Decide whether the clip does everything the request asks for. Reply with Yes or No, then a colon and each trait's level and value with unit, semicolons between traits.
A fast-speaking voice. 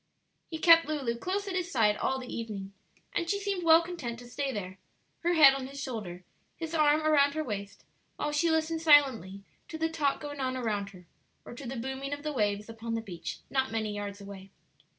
Yes: fast, 210 wpm